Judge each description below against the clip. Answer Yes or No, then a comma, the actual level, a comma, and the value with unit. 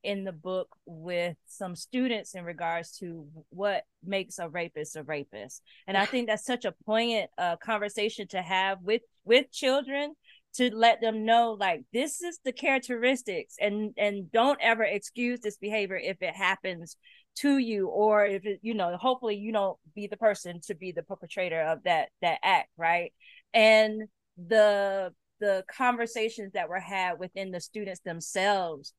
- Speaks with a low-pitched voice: No, high, 205 Hz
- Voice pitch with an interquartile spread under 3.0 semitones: No, average, 4.1 semitones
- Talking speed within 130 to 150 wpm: No, average, 170 wpm